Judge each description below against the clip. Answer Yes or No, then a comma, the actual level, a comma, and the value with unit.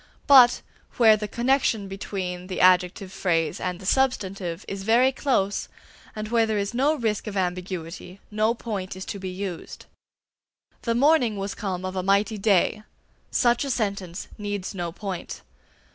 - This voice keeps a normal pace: Yes, average, 160 wpm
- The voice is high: Yes, high, 200 Hz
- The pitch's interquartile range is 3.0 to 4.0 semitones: Yes, average, 3.6 semitones